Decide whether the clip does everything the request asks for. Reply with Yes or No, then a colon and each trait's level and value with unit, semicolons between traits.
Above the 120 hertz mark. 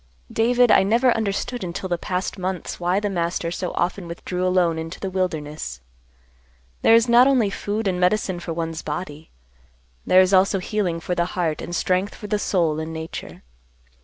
Yes: medium, 185 Hz